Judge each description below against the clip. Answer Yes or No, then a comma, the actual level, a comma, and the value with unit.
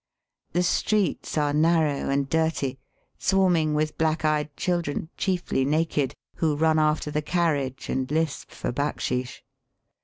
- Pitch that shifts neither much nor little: No, narrow, 2.2 semitones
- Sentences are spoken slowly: Yes, slow, 130 wpm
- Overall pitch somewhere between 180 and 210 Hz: No, medium, 155 Hz